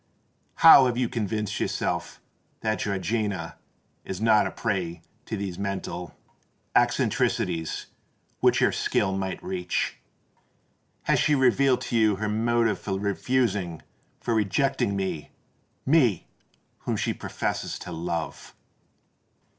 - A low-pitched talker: Yes, low, 100 Hz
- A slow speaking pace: Yes, slow, 110 wpm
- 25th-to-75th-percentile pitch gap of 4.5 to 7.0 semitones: No, average, 3.8 semitones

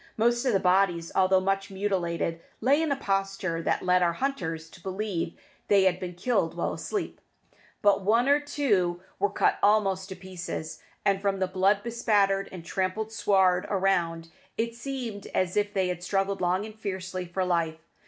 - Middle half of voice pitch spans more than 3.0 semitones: No, narrow, 2.5 semitones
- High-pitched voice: Yes, high, 195 Hz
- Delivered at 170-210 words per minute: Yes, average, 175 wpm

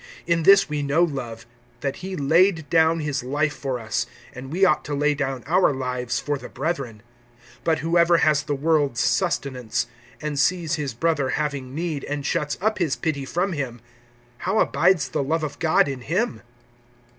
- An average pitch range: Yes, average, 3.7 semitones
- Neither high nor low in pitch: Yes, medium, 150 Hz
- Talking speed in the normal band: Yes, average, 180 wpm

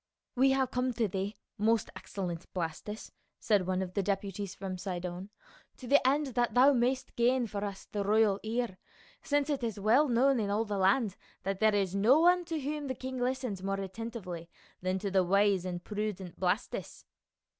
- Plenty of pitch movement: No, average, 4.6 semitones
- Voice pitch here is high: Yes, high, 210 Hz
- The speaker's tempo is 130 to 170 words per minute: No, average, 190 wpm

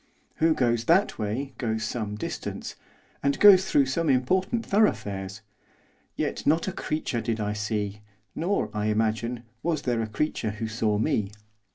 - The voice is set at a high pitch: No, low, 115 Hz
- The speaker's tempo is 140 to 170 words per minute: Yes, average, 155 wpm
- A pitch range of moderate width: No, wide, 6.5 semitones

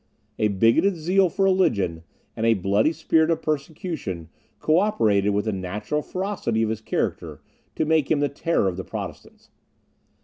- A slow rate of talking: No, average, 165 wpm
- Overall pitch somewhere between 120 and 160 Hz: Yes, medium, 140 Hz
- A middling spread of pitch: No, wide, 8.1 semitones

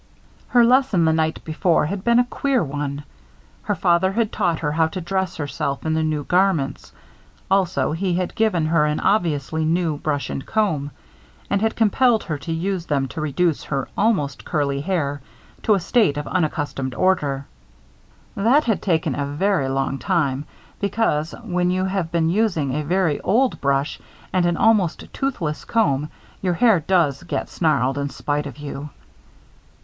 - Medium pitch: Yes, medium, 165 Hz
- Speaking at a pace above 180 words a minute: No, average, 170 wpm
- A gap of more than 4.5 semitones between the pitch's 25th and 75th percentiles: Yes, average, 4.9 semitones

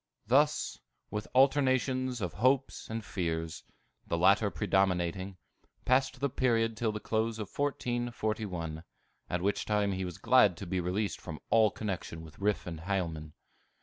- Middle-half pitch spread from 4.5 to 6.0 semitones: Yes, average, 5.2 semitones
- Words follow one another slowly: No, average, 150 wpm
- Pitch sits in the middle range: No, low, 105 Hz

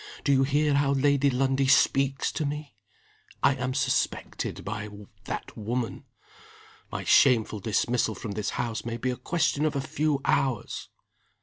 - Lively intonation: No, average, 3.1 semitones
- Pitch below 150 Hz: Yes, low, 135 Hz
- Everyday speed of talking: Yes, average, 150 wpm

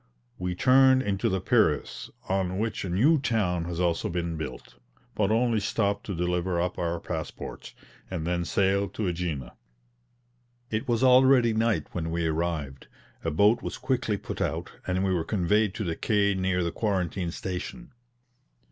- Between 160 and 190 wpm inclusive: Yes, average, 165 wpm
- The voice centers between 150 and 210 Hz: No, very low, 95 Hz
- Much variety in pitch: No, average, 4.2 semitones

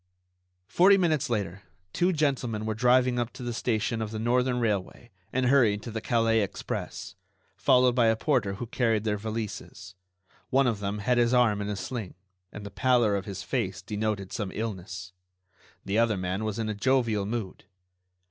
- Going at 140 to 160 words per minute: No, average, 180 wpm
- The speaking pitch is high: No, low, 110 Hz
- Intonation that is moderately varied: Yes, average, 3.1 semitones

